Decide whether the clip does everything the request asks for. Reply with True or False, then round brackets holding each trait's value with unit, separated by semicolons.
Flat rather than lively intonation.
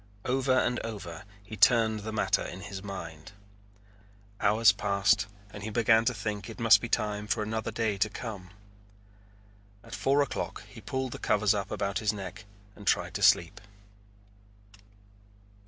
True (2.3 semitones)